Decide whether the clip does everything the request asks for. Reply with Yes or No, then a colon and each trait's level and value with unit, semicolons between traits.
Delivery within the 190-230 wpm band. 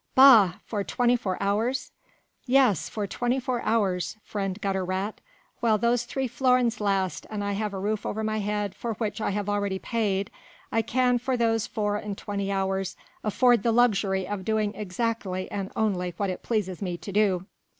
No: average, 180 wpm